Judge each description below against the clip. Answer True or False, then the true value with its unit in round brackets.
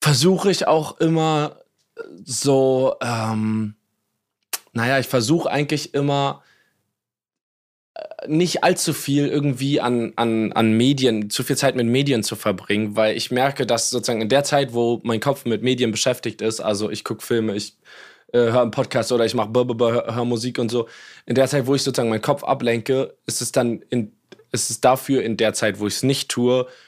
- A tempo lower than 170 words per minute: False (185 wpm)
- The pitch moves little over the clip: False (3.7 semitones)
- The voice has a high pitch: False (125 Hz)